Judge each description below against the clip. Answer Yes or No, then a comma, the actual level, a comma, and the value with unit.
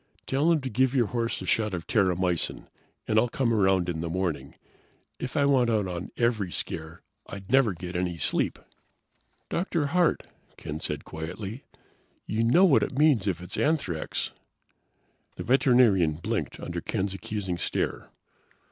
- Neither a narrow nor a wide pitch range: No, wide, 6.6 semitones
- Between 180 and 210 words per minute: No, average, 160 wpm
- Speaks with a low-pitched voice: Yes, low, 105 Hz